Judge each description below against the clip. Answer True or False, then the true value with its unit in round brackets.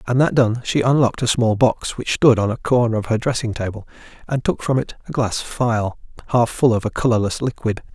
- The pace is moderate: False (225 wpm)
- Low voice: True (115 Hz)